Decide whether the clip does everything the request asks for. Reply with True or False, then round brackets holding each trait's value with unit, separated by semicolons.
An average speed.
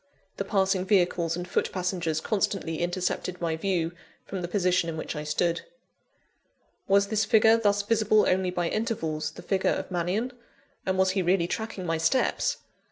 True (165 wpm)